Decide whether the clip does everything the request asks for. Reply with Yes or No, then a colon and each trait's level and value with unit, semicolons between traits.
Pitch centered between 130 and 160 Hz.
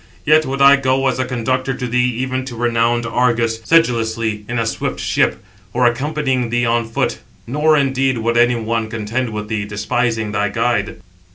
No: low, 120 Hz